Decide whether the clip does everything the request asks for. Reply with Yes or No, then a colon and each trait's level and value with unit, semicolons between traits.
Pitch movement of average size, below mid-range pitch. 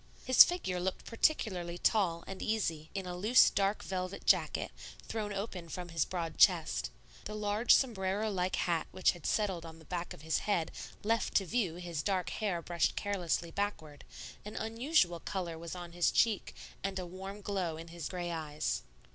No: average, 3.4 semitones; medium, 185 Hz